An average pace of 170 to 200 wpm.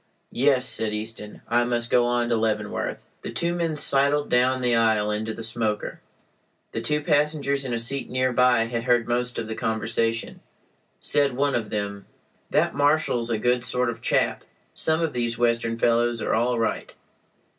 Yes: average, 175 wpm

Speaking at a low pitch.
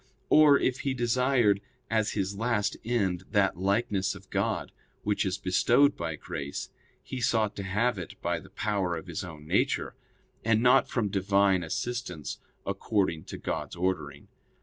Yes: low, 100 Hz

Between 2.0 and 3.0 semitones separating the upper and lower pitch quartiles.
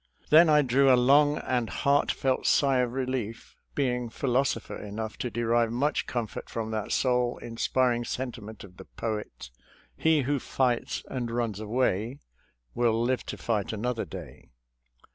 Yes: average, 2.7 semitones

